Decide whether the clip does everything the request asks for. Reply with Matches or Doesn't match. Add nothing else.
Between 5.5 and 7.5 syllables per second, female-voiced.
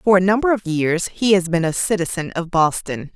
Doesn't match